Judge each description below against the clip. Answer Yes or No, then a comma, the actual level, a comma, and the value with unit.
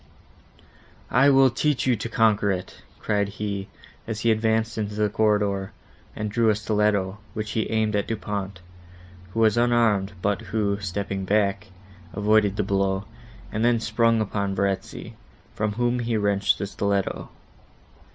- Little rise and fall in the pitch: Yes, narrow, 2.0 semitones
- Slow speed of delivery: No, average, 150 wpm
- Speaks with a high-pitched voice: No, low, 105 Hz